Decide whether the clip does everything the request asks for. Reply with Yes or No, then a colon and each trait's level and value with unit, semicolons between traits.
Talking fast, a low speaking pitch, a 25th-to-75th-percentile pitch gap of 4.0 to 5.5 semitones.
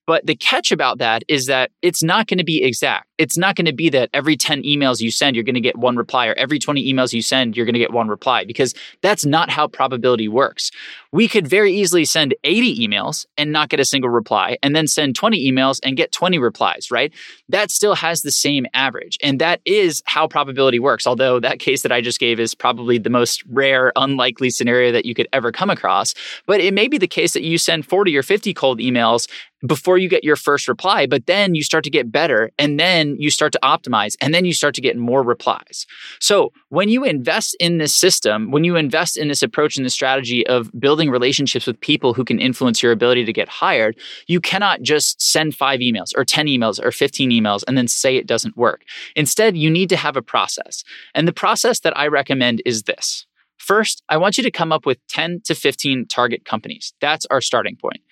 No: fast, 230 wpm; medium, 145 Hz; average, 4.8 semitones